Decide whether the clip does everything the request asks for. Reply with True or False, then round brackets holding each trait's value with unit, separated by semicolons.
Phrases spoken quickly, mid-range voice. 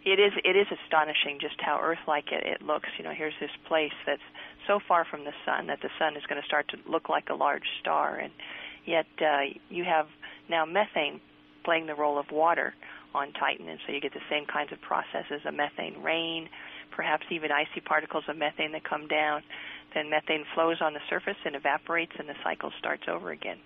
True (215 wpm; 155 Hz)